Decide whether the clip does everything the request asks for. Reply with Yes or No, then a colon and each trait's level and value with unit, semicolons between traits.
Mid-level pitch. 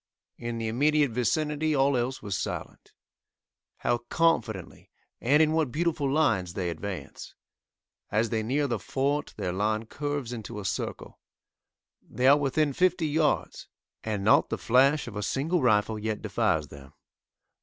No: low, 125 Hz